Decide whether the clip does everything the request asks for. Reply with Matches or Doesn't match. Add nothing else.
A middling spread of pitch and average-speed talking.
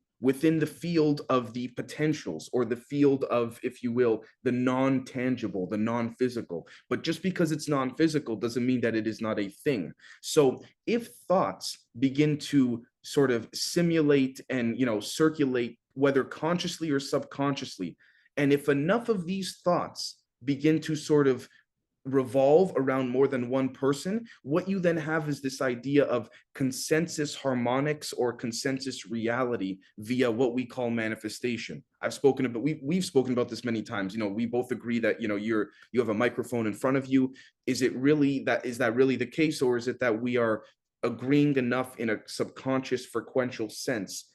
Matches